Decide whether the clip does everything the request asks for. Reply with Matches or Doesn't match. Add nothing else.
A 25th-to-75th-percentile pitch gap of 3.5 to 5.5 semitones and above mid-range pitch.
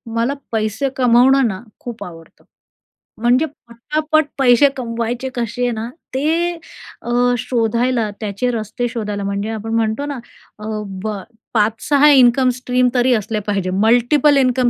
Doesn't match